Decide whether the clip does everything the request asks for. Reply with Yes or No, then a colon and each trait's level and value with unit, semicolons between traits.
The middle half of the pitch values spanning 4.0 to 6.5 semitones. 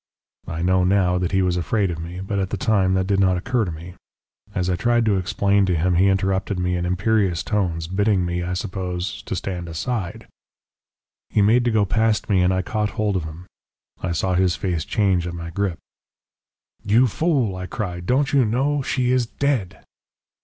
No: average, 3.2 semitones